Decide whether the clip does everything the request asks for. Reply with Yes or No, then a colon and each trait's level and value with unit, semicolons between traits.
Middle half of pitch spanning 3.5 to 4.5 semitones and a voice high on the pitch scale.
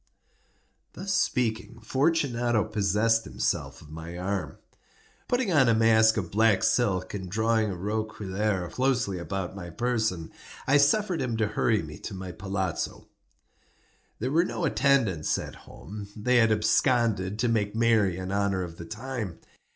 No: average, 4.1 semitones; low, 110 Hz